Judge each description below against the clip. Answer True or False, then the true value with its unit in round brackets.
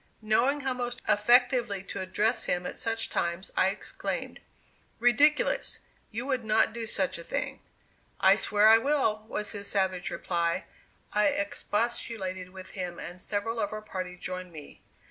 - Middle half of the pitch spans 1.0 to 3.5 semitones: False (4.1 semitones)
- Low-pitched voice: False (210 Hz)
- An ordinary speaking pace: True (155 wpm)